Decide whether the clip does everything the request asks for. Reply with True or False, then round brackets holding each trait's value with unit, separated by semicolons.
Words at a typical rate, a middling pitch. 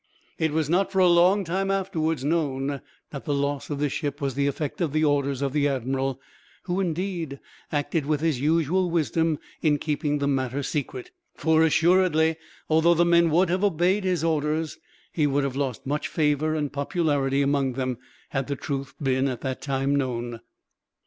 True (180 wpm; 150 Hz)